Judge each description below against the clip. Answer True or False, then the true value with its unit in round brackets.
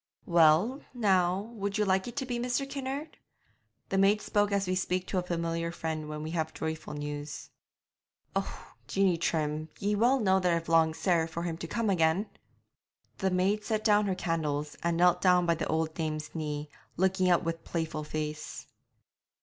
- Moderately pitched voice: True (175 Hz)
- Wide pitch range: False (3.8 semitones)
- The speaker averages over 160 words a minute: True (180 wpm)